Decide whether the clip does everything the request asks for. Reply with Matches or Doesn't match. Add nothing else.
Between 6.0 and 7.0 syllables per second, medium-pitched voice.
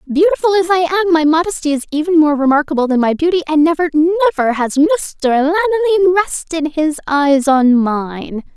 Doesn't match